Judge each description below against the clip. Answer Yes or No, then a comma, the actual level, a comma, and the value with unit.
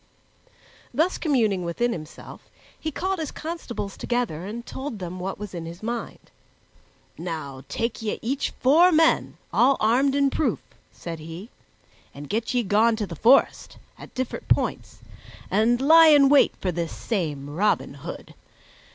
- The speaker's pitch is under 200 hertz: No, high, 225 Hz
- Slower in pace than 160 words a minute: Yes, average, 150 wpm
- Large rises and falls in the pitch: Yes, wide, 7.3 semitones